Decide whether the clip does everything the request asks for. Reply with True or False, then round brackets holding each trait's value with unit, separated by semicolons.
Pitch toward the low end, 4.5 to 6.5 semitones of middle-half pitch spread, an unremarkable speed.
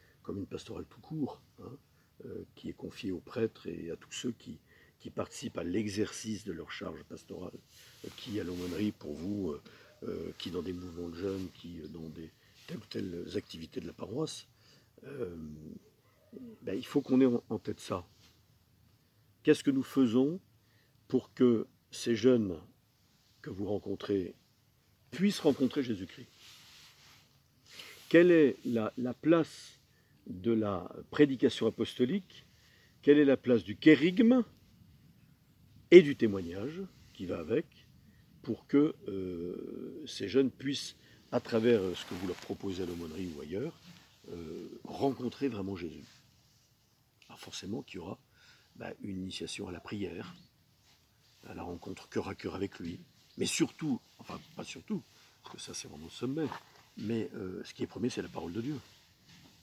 True (115 Hz; 5.4 semitones; 155 wpm)